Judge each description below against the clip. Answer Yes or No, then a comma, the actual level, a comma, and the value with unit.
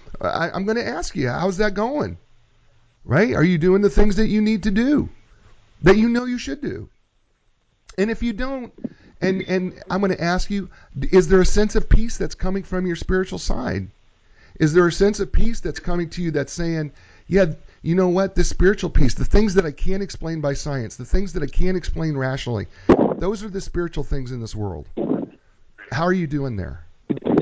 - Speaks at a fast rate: Yes, fast, 210 wpm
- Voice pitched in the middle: Yes, medium, 175 Hz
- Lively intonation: Yes, wide, 7.5 semitones